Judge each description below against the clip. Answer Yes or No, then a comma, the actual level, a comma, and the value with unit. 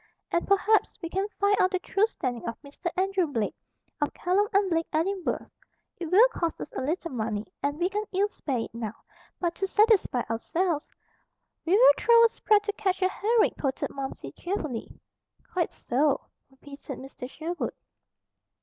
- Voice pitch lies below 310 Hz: No, very high, 345 Hz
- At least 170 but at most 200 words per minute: Yes, average, 175 wpm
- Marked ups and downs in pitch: Yes, wide, 6.1 semitones